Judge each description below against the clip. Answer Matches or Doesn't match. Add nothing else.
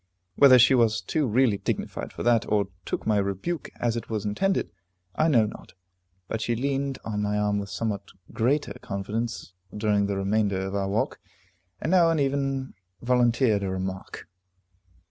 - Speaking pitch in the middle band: Doesn't match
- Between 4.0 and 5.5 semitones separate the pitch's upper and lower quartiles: Matches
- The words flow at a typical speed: Matches